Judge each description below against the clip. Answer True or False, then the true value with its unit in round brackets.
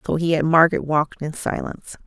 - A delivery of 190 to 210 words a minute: True (205 wpm)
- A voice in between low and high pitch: True (160 Hz)